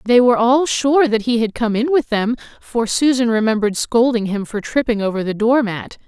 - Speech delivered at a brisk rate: Yes, fast, 215 wpm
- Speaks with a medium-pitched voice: No, high, 235 Hz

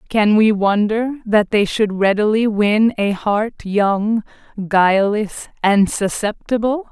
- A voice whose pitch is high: Yes, high, 210 Hz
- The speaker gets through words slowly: Yes, slow, 120 wpm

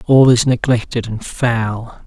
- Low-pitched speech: Yes, low, 115 Hz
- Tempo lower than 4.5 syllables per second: Yes, 3.7 syllables/s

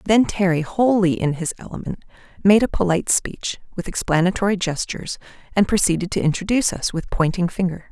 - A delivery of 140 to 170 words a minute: Yes, average, 160 wpm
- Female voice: Yes, female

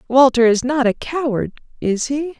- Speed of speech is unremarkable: Yes, average, 175 wpm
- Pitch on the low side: No, very high, 260 Hz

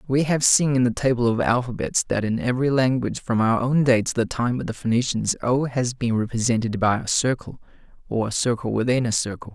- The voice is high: No, low, 120 Hz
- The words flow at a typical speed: No, fast, 220 wpm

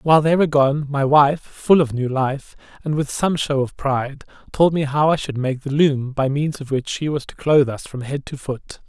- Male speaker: Yes, male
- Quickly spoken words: Yes, fast, 250 wpm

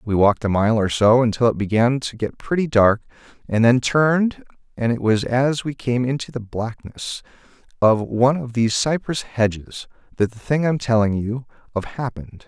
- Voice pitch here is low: Yes, low, 120 Hz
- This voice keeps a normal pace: Yes, average, 190 wpm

